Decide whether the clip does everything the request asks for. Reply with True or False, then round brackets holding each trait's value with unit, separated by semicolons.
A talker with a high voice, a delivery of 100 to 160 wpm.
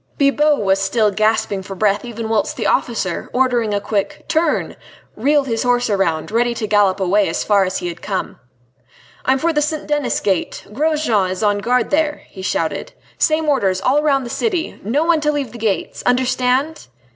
False (235 Hz; 190 wpm)